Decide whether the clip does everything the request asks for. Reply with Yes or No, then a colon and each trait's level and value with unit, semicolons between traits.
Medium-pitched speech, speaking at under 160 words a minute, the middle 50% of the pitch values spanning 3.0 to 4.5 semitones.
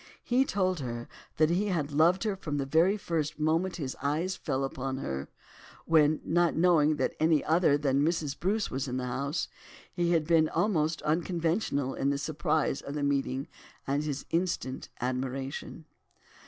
No: medium, 155 Hz; average, 170 wpm; average, 3.7 semitones